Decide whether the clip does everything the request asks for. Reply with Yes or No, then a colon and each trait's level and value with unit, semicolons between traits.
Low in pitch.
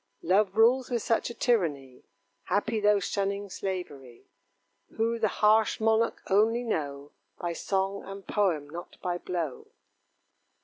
No: high, 200 Hz